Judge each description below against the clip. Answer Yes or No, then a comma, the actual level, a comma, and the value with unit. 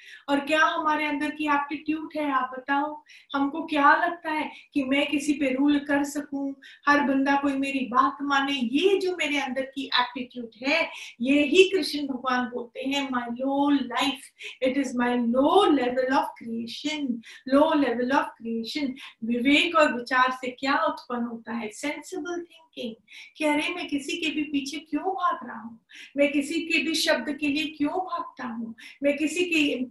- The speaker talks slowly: No, average, 175 wpm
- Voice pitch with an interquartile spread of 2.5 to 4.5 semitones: Yes, average, 2.8 semitones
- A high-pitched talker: Yes, very high, 285 Hz